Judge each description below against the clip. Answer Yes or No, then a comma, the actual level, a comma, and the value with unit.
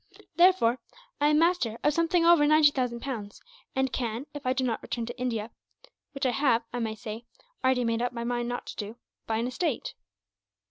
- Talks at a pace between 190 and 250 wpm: Yes, average, 200 wpm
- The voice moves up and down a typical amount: Yes, average, 4.0 semitones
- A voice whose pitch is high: Yes, very high, 250 Hz